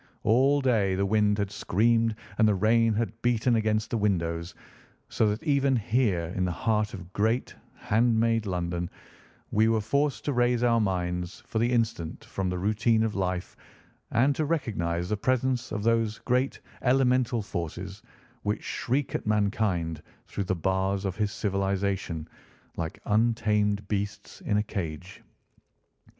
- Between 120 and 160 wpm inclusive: Yes, average, 155 wpm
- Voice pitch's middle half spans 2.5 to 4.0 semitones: Yes, average, 3.5 semitones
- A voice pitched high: No, low, 105 Hz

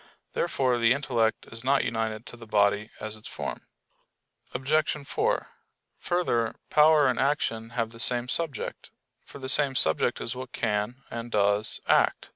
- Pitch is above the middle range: No, low, 120 Hz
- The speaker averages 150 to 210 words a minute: Yes, average, 155 wpm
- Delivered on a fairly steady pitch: No, average, 3.4 semitones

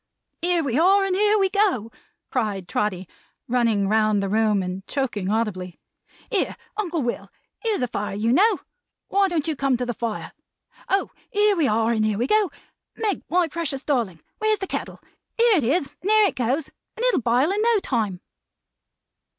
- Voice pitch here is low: No, very high, 270 Hz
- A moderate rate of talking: Yes, average, 185 wpm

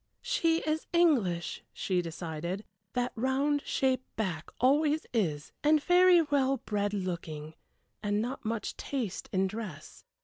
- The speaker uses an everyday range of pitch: No, wide, 7.9 semitones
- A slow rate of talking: Yes, slow, 130 wpm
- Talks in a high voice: Yes, high, 230 Hz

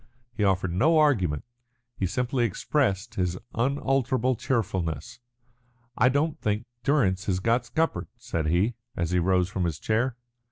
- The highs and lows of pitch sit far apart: Yes, wide, 5.9 semitones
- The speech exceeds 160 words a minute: No, average, 150 wpm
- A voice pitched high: No, low, 110 Hz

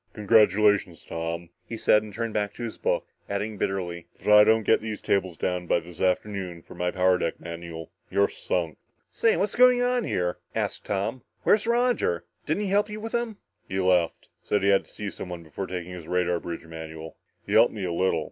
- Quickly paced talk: Yes, fast, 210 wpm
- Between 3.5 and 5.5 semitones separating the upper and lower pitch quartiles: Yes, average, 4.2 semitones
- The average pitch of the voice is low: Yes, very low, 95 Hz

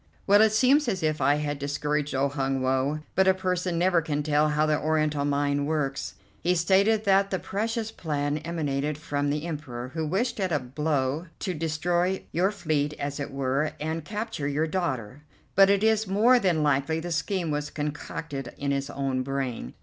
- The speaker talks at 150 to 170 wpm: No, average, 190 wpm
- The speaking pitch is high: No, medium, 155 Hz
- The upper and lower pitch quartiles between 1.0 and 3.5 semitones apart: No, average, 4.5 semitones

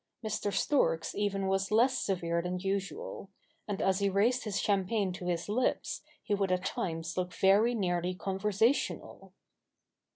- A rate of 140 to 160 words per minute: Yes, average, 150 wpm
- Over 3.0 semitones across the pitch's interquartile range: No, narrow, 2.6 semitones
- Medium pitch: No, high, 195 Hz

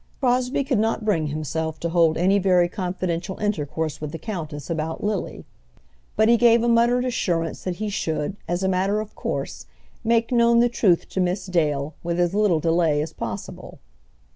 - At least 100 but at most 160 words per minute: No, average, 180 wpm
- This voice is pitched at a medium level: Yes, medium, 180 Hz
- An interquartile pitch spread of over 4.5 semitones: Yes, average, 5.1 semitones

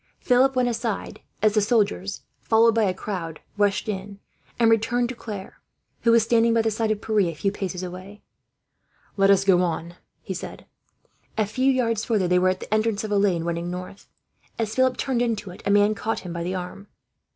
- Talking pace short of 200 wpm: No, fast, 205 wpm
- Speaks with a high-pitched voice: Yes, high, 205 Hz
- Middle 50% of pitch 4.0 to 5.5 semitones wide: No, average, 3.5 semitones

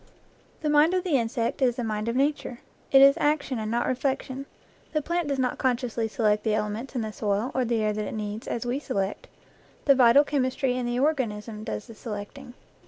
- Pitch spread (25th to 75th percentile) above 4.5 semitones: No, average, 4.0 semitones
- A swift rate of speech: Yes, fast, 215 wpm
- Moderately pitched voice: No, high, 245 Hz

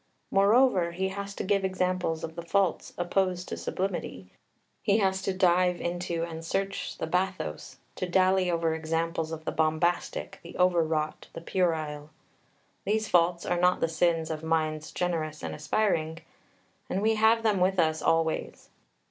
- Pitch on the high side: No, medium, 175 Hz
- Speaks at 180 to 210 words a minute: No, average, 160 wpm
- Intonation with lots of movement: No, average, 2.9 semitones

